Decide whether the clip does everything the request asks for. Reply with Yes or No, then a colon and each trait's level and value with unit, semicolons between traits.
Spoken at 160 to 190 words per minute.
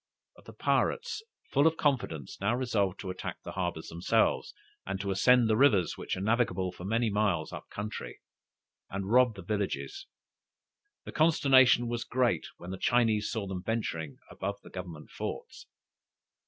Yes: average, 165 wpm